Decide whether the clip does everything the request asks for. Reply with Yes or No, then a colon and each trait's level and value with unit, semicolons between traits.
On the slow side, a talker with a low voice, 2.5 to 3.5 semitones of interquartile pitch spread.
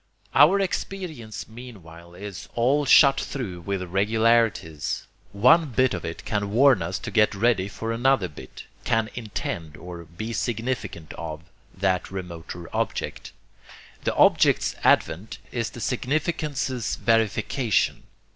No: slow, 125 wpm; low, 110 Hz; wide, 5.6 semitones